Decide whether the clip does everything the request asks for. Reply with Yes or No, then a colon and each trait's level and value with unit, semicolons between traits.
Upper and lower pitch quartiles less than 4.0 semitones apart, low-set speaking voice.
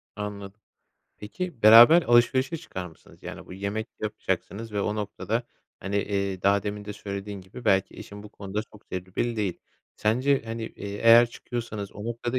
Yes: average, 2.7 semitones; low, 105 Hz